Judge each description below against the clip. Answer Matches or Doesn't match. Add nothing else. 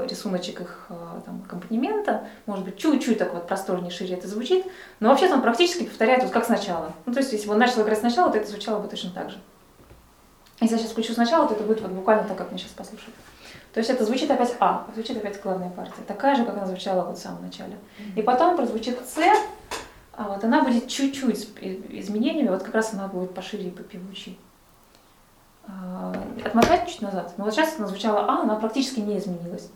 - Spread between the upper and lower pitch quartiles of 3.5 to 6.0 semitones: Matches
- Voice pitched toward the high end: Matches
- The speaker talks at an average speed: Doesn't match